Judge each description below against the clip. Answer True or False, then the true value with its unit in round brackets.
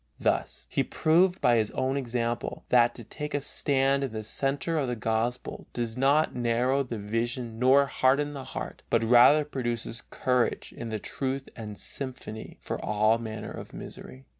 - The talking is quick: False (170 wpm)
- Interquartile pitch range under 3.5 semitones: True (3.1 semitones)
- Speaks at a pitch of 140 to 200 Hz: False (125 Hz)